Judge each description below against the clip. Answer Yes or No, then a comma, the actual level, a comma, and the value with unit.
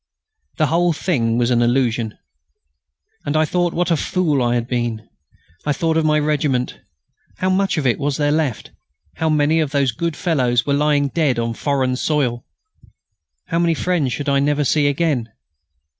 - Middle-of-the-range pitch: Yes, medium, 145 Hz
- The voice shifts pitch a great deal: No, average, 4.3 semitones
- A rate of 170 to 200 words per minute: Yes, average, 175 wpm